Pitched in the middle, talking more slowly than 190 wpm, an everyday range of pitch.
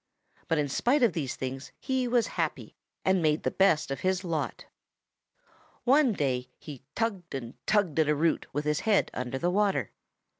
No: medium, 165 Hz; average, 175 wpm; wide, 6.4 semitones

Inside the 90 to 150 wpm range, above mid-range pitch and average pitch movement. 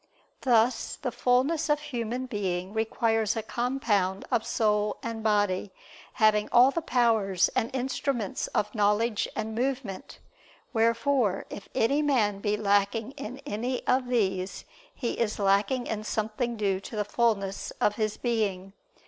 Yes: average, 140 wpm; high, 225 Hz; average, 3.1 semitones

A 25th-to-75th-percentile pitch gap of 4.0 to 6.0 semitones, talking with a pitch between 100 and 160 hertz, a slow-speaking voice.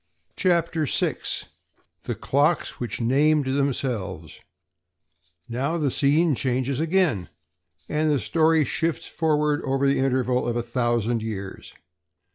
Yes: average, 4.3 semitones; low, 135 Hz; slow, 115 wpm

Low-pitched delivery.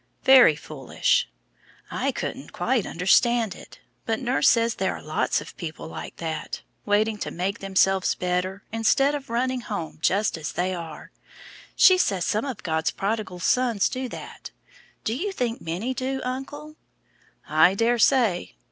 No: high, 215 Hz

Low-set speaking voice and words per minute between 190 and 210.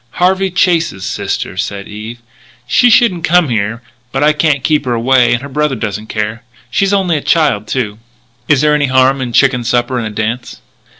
Yes: low, 130 Hz; average, 195 wpm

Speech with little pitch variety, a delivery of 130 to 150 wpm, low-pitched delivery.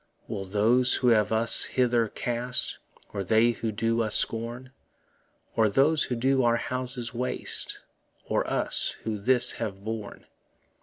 Yes: narrow, 2.3 semitones; average, 145 wpm; low, 115 Hz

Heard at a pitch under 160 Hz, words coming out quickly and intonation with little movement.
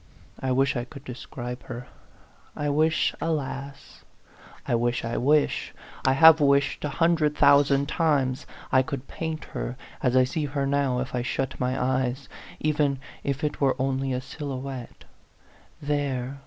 No: low, 135 Hz; average, 155 wpm; narrow, 2.3 semitones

